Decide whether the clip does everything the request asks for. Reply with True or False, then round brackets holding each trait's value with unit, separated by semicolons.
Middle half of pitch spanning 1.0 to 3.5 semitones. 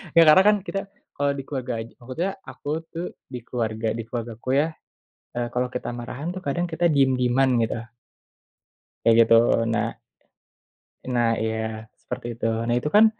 False (4.0 semitones)